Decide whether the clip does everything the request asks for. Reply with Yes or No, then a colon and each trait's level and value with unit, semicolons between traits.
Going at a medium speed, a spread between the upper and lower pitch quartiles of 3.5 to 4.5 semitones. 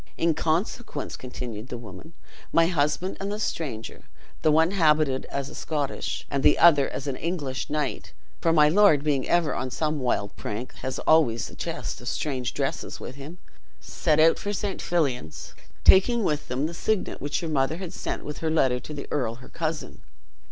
Yes: average, 185 wpm; average, 4.1 semitones